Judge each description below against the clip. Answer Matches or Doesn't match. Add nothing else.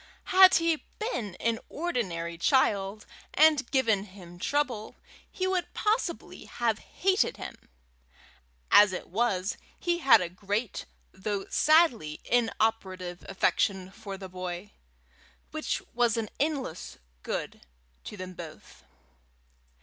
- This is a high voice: Matches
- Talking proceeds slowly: Matches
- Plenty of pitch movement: Matches